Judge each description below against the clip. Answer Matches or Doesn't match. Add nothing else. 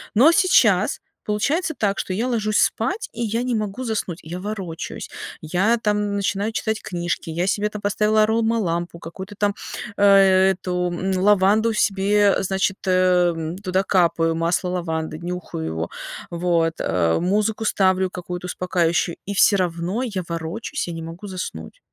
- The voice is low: Doesn't match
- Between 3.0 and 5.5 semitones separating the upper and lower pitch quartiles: Matches